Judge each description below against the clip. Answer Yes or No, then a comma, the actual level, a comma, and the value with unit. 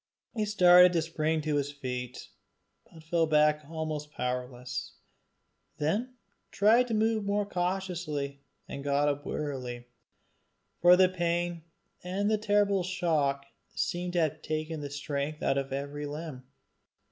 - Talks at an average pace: No, slow, 130 wpm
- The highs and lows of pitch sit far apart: No, average, 4.0 semitones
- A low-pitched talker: No, medium, 155 Hz